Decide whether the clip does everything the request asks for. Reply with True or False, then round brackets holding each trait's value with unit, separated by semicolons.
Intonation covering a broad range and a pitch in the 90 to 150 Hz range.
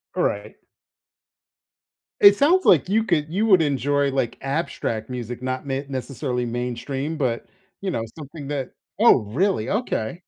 True (5.7 semitones; 140 Hz)